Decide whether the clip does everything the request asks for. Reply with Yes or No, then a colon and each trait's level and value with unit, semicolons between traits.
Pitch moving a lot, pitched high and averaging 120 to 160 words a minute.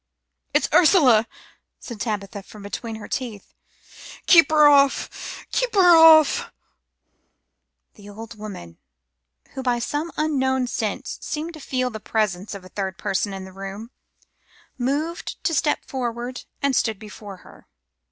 Yes: wide, 6.1 semitones; high, 235 Hz; average, 140 wpm